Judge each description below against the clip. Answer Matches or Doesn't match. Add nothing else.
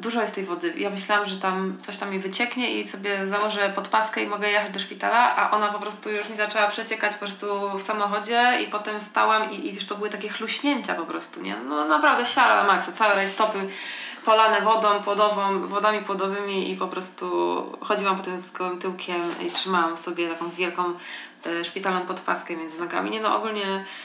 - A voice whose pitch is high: Matches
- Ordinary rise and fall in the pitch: Doesn't match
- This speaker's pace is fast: Matches